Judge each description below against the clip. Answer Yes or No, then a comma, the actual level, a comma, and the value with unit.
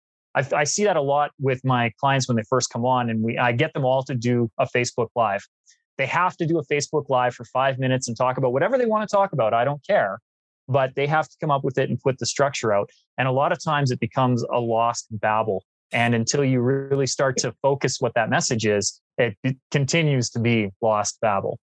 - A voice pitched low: Yes, low, 130 Hz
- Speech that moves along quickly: Yes, fast, 240 wpm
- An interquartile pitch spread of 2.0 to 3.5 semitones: Yes, average, 3.1 semitones